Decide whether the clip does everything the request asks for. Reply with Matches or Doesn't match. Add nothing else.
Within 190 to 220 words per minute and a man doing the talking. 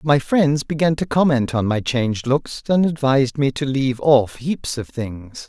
Matches